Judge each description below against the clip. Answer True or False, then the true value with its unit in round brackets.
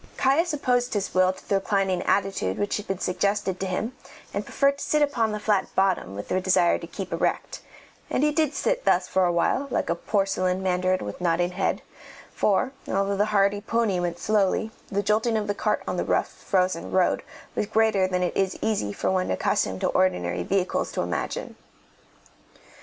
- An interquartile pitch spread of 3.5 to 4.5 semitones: False (2.9 semitones)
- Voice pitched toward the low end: False (195 Hz)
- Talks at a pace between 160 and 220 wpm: True (190 wpm)